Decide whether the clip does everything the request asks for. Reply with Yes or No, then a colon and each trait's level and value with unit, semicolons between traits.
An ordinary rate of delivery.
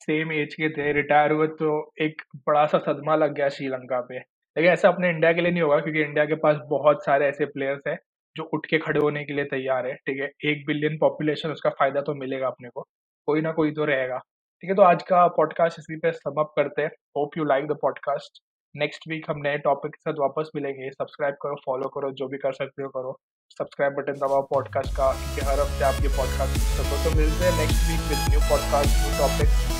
No: fast, 225 wpm